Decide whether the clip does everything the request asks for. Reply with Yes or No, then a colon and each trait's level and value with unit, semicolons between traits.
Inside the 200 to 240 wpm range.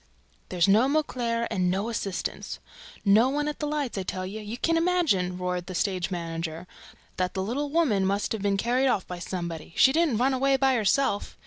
Yes: fast, 205 wpm